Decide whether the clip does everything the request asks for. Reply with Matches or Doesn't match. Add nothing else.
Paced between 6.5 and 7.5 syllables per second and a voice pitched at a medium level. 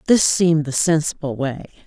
Doesn't match